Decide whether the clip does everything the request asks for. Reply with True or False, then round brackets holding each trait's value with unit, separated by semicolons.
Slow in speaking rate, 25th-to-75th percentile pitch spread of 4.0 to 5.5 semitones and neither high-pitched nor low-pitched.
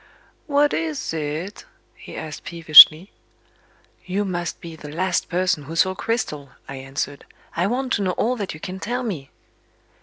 False (160 wpm; 4.6 semitones; 175 Hz)